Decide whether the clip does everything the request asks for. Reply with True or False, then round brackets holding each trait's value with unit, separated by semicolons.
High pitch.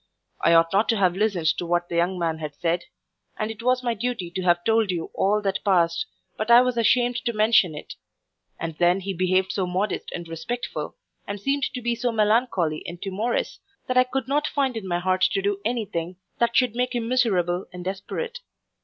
True (200 Hz)